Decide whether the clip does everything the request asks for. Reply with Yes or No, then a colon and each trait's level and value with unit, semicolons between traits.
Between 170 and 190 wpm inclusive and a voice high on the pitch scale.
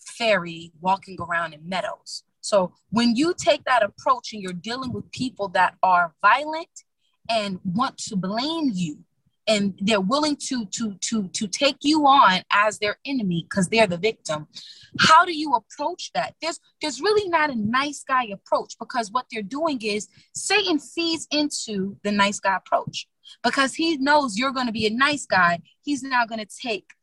Yes: average, 180 wpm; high, 235 Hz